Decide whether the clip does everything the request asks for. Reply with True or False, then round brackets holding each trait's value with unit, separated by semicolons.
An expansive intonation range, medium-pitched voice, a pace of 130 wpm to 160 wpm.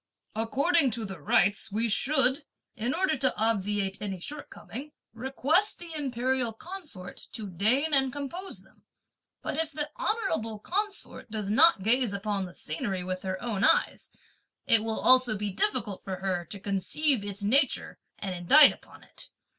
False (6.3 semitones; 225 Hz; 155 wpm)